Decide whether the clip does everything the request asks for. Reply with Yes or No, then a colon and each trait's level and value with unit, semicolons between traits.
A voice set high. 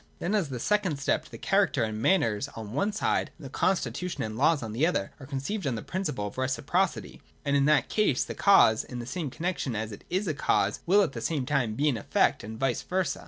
No: medium, 140 Hz